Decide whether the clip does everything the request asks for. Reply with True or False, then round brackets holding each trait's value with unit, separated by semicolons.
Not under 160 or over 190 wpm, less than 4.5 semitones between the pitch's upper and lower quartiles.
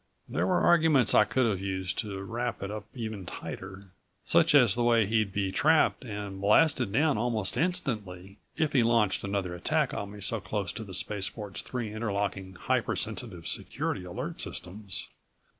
True (170 wpm; 3.8 semitones)